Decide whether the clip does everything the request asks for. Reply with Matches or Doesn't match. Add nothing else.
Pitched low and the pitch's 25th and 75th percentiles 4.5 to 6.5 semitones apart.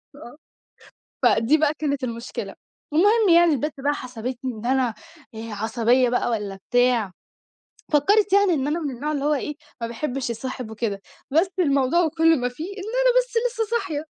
Doesn't match